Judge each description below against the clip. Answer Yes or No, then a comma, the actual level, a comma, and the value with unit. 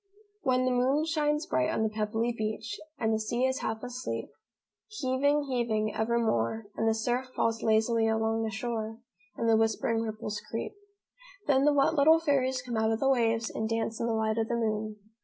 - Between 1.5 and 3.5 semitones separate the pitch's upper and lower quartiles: Yes, average, 2.7 semitones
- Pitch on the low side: No, high, 225 Hz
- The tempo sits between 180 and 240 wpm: Yes, average, 195 wpm